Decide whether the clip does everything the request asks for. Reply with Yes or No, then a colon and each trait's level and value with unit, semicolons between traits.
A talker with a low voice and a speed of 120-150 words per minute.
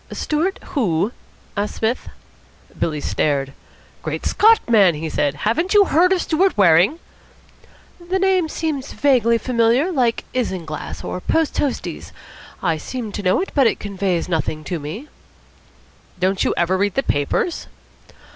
No: high, 225 Hz; average, 145 wpm